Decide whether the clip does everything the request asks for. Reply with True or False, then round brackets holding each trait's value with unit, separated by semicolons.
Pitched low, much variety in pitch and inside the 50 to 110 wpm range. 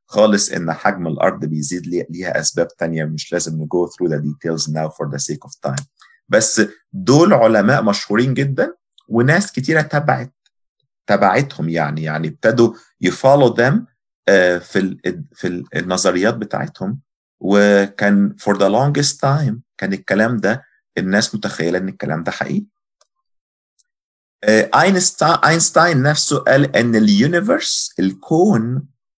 False (105 Hz; 8.8 semitones; 120 wpm)